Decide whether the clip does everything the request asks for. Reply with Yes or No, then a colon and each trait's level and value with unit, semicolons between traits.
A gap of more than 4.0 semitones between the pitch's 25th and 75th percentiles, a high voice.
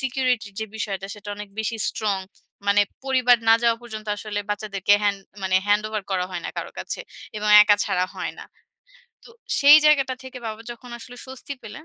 No: average, 3.4 semitones; high, 215 Hz